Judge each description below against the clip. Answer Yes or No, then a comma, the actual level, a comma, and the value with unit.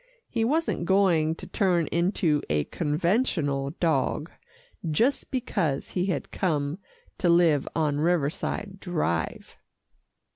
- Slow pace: Yes, slow, 110 wpm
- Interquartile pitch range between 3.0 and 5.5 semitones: Yes, average, 4.4 semitones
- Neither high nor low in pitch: Yes, medium, 170 Hz